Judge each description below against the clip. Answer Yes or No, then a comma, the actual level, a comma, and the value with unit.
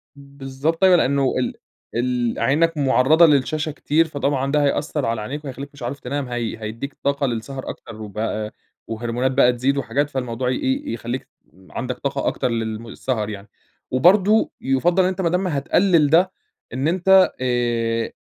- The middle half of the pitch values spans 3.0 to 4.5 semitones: Yes, average, 4.2 semitones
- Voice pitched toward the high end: No, low, 135 Hz